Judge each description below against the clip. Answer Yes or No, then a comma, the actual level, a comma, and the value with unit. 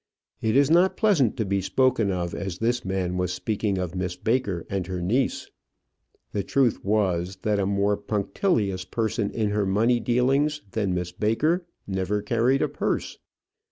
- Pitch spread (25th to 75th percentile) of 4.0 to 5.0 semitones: Yes, average, 4.4 semitones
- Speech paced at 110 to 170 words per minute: Yes, average, 165 wpm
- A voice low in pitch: Yes, low, 105 Hz